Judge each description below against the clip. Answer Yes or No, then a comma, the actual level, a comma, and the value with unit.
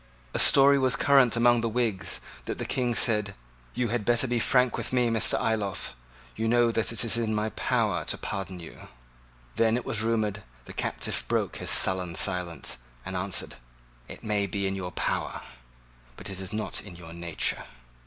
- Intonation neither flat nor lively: Yes, average, 3.7 semitones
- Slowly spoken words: No, average, 185 wpm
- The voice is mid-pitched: No, low, 110 Hz